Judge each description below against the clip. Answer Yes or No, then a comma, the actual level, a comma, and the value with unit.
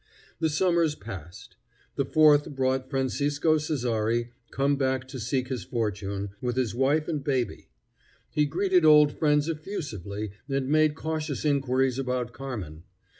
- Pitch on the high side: No, low, 135 Hz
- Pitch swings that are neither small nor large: Yes, average, 3.8 semitones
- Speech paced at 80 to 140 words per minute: Yes, slow, 135 wpm